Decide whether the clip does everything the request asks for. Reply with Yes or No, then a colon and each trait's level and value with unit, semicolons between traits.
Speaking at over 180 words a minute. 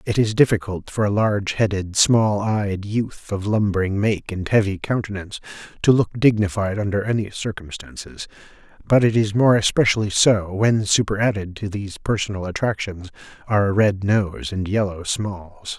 No: average, 155 wpm